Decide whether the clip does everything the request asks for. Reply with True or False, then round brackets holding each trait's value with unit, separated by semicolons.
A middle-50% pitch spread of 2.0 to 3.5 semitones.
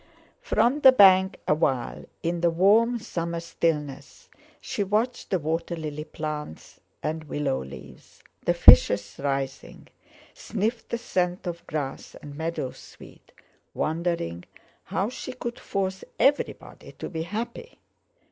False (5.3 semitones)